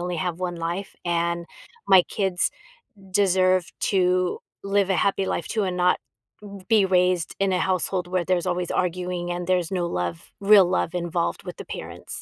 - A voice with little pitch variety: Yes, narrow, 1.2 semitones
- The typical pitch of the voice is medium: Yes, medium, 180 Hz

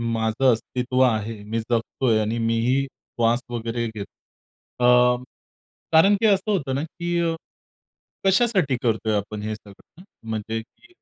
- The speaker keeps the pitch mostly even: No, average, 3.6 semitones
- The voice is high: No, low, 120 Hz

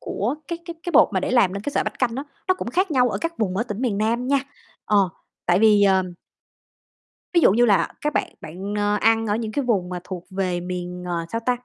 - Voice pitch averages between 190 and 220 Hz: Yes, high, 210 Hz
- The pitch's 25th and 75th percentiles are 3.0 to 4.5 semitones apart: No, average, 5.0 semitones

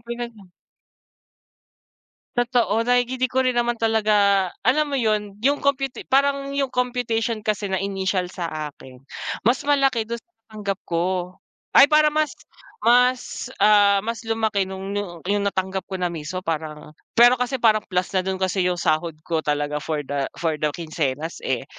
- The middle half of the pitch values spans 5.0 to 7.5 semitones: Yes, wide, 5.6 semitones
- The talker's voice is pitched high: Yes, high, 205 Hz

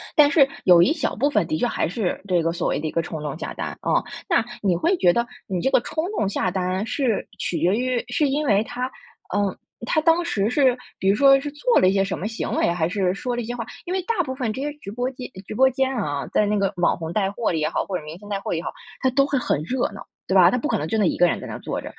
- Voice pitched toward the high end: Yes, high, 215 Hz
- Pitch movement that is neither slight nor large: No, wide, 6.5 semitones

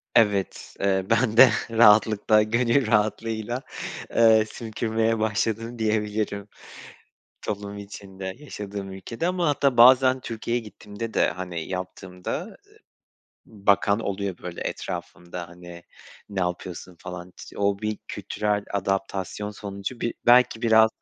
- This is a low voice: Yes, low, 105 Hz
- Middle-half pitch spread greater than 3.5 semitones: No, average, 2.7 semitones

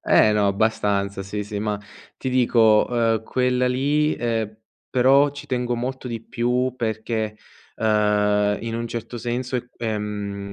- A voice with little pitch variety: No, average, 3.0 semitones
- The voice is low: Yes, low, 115 Hz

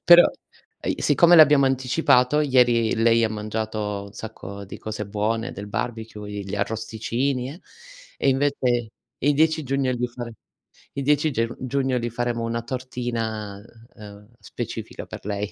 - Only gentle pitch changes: No, average, 3.7 semitones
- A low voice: Yes, low, 115 Hz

